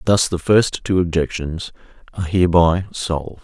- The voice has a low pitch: Yes, very low, 90 Hz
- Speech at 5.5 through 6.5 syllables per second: No, 5.0 syllables/s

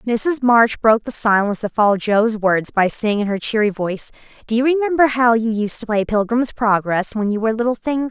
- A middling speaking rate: No, fast, 220 wpm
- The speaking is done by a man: No, female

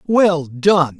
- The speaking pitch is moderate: Yes, medium, 165 Hz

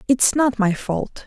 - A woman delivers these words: Yes, female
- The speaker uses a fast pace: No, average, 190 wpm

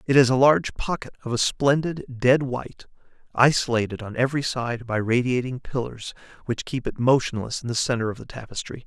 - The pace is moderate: Yes, average, 185 wpm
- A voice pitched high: No, low, 125 Hz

